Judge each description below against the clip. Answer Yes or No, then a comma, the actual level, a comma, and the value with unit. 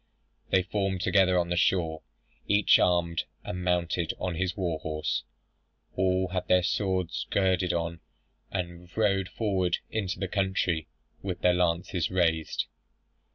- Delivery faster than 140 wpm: No, slow, 135 wpm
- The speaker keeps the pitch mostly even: Yes, narrow, 1.6 semitones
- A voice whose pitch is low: Yes, very low, 90 Hz